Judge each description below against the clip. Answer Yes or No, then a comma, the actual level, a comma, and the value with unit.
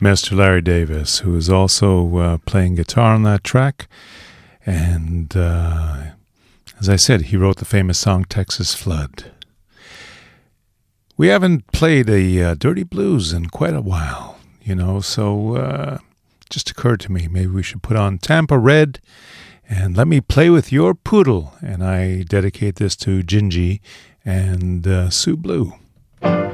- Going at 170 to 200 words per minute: No, average, 150 wpm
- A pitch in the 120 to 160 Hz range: No, very low, 95 Hz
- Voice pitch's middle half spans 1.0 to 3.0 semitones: No, average, 4.3 semitones